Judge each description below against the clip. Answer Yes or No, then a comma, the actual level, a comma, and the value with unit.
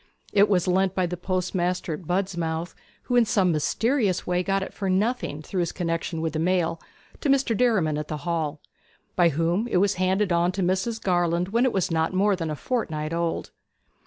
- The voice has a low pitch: No, medium, 180 Hz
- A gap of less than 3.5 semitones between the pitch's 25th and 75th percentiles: Yes, average, 2.9 semitones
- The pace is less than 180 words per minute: No, average, 200 wpm